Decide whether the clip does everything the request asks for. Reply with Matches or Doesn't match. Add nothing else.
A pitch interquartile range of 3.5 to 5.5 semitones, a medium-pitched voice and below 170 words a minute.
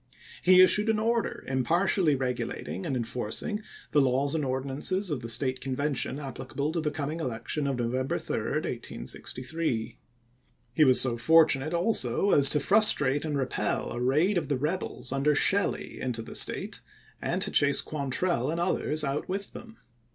Matches